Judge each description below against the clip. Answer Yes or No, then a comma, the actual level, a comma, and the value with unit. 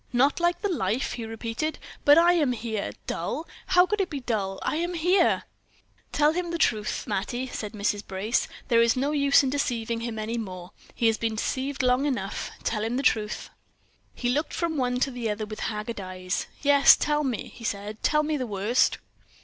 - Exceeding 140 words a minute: Yes, average, 200 wpm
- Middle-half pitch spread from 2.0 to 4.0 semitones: No, wide, 5.4 semitones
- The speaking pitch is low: No, high, 245 Hz